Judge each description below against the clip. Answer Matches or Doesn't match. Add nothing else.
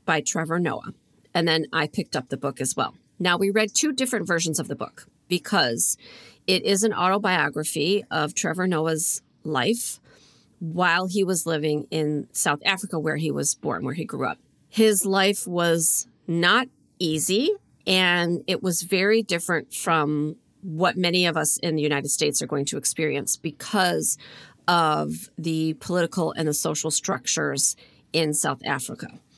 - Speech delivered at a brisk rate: Doesn't match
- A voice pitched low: Doesn't match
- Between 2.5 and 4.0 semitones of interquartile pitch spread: Matches